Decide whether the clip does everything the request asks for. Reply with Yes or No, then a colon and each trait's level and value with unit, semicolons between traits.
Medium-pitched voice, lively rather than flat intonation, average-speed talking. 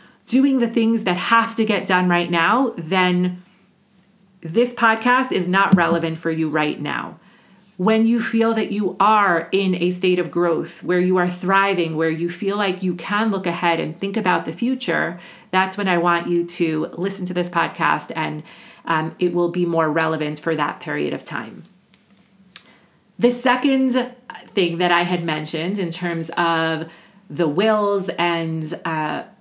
No: medium, 180 Hz; average, 3.2 semitones; average, 170 wpm